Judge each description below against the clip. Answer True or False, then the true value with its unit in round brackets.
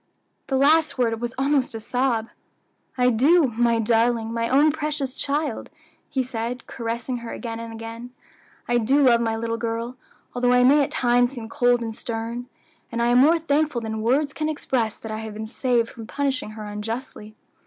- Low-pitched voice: False (240 Hz)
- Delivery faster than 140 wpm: True (185 wpm)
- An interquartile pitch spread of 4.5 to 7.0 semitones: False (2.9 semitones)